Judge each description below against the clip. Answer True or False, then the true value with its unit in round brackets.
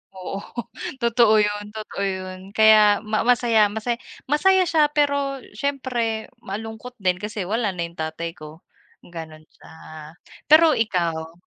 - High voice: True (215 Hz)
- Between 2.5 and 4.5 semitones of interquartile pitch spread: False (5.2 semitones)